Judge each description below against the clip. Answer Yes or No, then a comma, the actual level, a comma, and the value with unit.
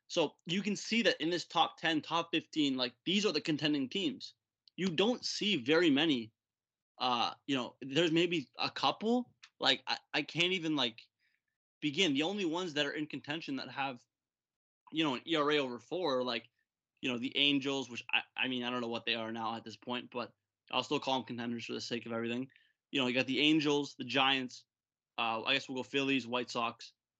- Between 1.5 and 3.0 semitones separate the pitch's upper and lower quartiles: No, average, 4.5 semitones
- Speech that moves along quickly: Yes, fast, 215 wpm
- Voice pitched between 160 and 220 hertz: No, low, 135 Hz